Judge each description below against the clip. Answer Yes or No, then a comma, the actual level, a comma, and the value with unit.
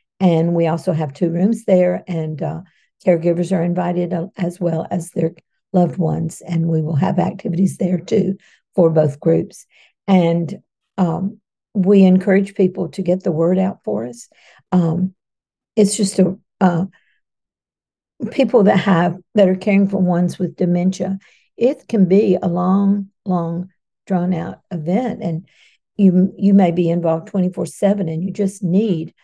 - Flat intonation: Yes, narrow, 2.3 semitones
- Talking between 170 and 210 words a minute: No, average, 155 wpm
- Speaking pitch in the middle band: Yes, medium, 180 Hz